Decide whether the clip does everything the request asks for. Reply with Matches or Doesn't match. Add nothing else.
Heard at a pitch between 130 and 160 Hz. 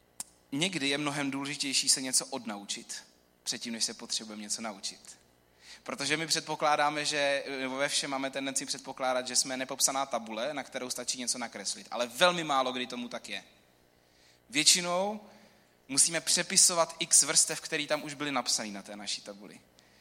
Matches